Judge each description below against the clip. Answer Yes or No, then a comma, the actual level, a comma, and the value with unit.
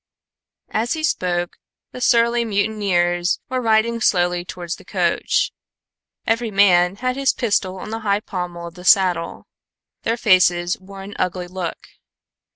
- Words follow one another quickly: No, average, 145 wpm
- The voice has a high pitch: Yes, high, 195 Hz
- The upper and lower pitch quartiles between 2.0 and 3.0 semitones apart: No, average, 4.3 semitones